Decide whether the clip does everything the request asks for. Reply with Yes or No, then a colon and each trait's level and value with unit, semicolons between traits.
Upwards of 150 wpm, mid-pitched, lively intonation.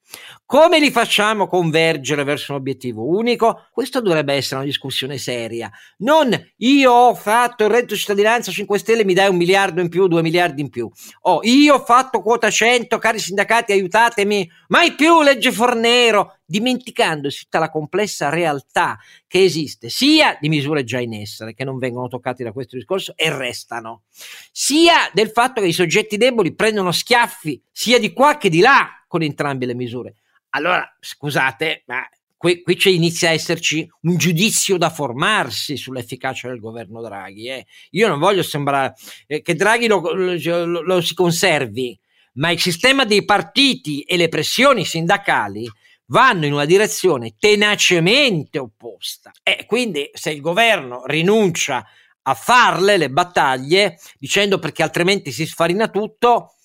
Yes: average, 160 wpm; medium, 175 Hz; wide, 7.1 semitones